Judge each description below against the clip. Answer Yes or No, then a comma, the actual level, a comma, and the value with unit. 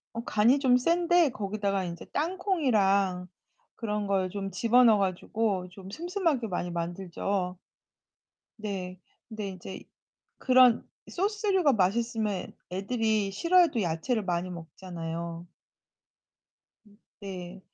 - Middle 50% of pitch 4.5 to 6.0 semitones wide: Yes, average, 5.3 semitones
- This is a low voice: No, high, 205 Hz